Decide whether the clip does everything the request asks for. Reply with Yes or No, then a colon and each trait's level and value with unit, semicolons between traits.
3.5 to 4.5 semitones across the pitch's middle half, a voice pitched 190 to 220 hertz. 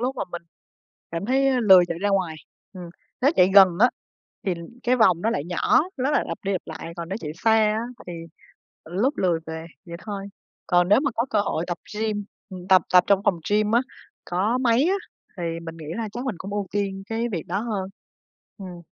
Yes: average, 4.2 semitones; high, 195 Hz